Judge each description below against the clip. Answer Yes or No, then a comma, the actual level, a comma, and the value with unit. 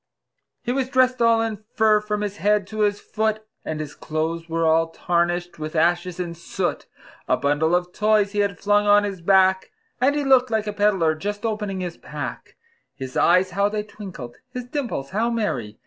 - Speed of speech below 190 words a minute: No, average, 195 wpm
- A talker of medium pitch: No, high, 200 Hz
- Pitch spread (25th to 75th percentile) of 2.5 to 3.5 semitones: No, average, 4.2 semitones